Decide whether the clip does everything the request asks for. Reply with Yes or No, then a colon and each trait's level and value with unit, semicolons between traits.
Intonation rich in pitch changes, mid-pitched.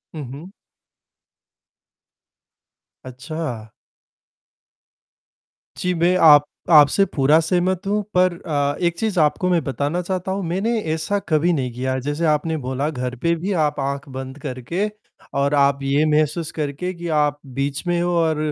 No: average, 3.9 semitones; medium, 155 Hz